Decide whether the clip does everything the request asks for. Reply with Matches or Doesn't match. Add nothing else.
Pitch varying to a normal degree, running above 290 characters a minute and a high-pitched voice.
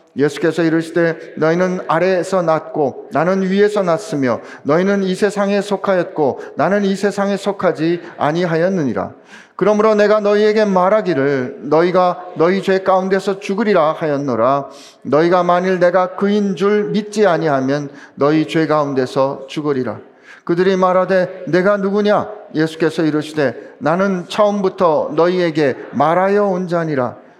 Doesn't match